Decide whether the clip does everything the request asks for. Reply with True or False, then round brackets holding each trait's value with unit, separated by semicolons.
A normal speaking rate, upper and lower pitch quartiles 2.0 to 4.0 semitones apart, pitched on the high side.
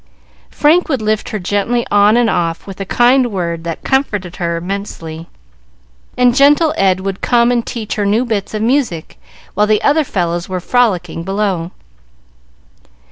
False (160 wpm; 5.2 semitones; 205 Hz)